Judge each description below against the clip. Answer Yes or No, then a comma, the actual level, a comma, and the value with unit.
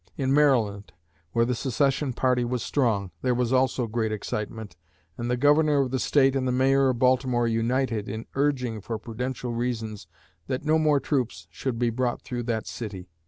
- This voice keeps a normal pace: Yes, average, 180 wpm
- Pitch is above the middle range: No, low, 125 Hz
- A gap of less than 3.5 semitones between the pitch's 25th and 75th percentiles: Yes, average, 2.7 semitones